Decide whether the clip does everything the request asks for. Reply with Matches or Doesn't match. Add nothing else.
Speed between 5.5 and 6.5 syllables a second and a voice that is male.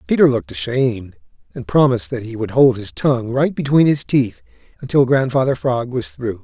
Matches